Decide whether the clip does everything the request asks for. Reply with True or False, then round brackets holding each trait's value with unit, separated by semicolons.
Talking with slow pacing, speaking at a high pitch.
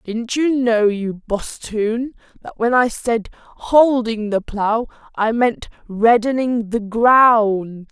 True (130 wpm; 230 Hz)